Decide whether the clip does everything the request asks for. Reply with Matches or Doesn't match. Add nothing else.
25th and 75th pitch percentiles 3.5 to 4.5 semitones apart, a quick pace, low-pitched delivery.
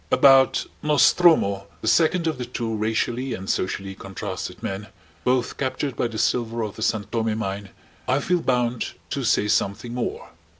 Doesn't match